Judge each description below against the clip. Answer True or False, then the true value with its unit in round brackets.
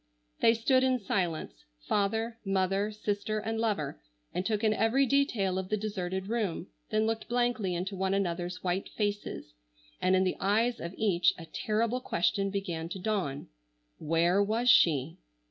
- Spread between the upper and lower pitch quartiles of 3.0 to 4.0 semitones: True (3.4 semitones)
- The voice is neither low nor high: False (200 Hz)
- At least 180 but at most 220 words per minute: False (160 wpm)